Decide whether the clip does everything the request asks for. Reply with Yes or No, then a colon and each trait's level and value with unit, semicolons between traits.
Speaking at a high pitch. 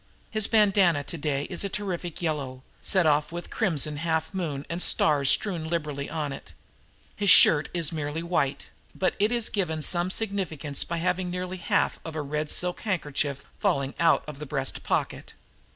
No: medium, 165 Hz